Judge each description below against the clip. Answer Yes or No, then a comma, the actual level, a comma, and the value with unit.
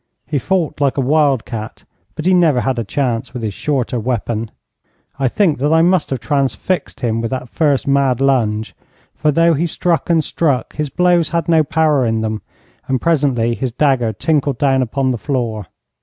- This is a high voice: No, low, 135 Hz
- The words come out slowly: No, average, 190 wpm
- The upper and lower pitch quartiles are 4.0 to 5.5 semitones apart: Yes, average, 4.6 semitones